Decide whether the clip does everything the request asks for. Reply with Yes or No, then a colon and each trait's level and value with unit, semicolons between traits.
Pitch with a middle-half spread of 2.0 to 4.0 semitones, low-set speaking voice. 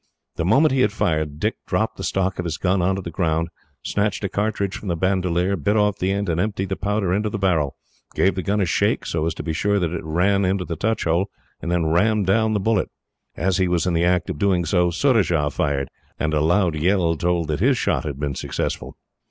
Yes: average, 3.4 semitones; very low, 90 Hz